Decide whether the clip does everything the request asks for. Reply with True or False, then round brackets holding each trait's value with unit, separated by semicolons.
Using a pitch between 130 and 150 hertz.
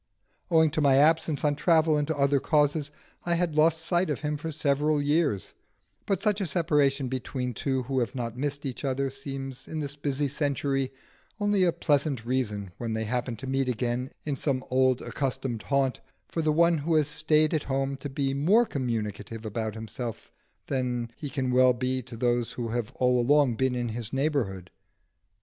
True (135 Hz)